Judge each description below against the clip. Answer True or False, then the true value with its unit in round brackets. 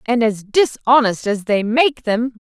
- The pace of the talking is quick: False (175 wpm)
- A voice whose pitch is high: True (235 Hz)